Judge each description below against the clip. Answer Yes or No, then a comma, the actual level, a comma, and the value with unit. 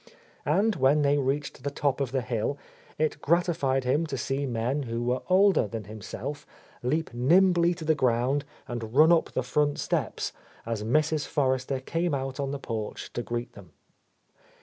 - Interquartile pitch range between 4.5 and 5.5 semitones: No, average, 4.0 semitones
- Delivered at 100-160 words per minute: No, average, 170 wpm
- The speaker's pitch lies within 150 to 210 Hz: No, low, 135 Hz